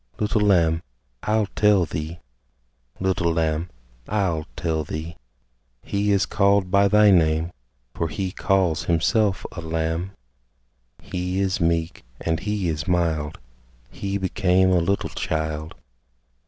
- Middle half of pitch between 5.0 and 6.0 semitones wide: No, average, 3.4 semitones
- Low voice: Yes, very low, 90 Hz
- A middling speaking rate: No, slow, 125 wpm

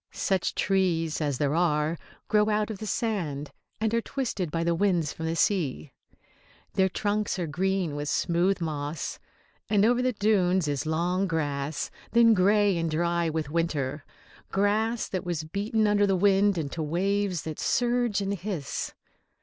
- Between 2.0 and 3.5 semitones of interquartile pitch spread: No, average, 4.3 semitones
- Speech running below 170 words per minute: Yes, average, 160 wpm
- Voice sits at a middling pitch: Yes, medium, 180 Hz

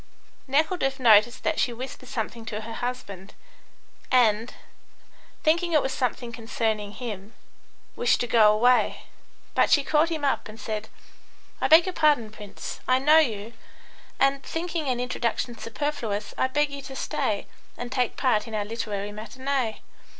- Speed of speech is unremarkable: Yes, average, 155 wpm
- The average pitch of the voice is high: Yes, high, 245 Hz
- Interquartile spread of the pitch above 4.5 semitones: No, average, 4.1 semitones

